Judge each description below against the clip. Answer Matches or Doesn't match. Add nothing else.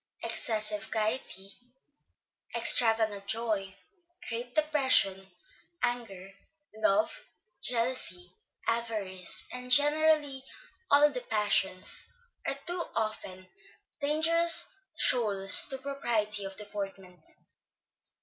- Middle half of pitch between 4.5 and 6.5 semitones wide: Matches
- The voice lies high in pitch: Matches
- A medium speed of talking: Doesn't match